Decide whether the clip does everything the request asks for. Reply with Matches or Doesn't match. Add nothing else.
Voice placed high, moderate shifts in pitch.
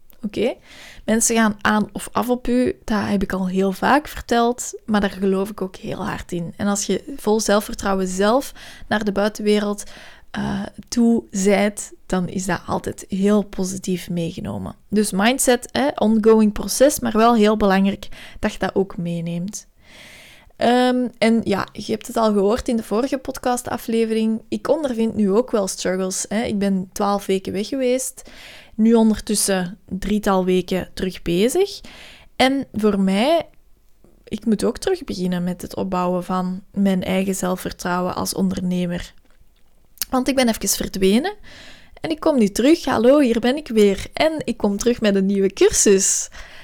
Matches